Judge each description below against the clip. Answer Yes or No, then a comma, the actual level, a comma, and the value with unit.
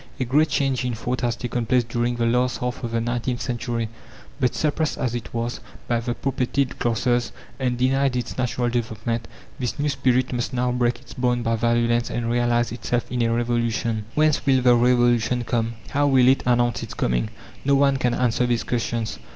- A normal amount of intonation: No, narrow, 1.2 semitones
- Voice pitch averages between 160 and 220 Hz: No, low, 120 Hz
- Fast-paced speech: No, average, 195 wpm